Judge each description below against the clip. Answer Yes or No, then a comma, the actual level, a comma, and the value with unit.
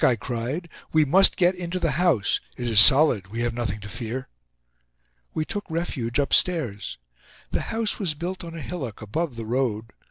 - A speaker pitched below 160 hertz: Yes, low, 135 Hz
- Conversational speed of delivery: Yes, average, 170 wpm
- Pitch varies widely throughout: Yes, wide, 6.8 semitones